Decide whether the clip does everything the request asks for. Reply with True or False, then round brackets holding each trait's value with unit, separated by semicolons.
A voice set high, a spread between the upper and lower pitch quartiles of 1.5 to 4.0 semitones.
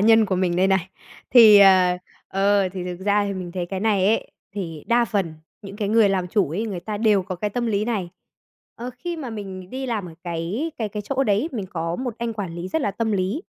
True (200 Hz; 3.2 semitones)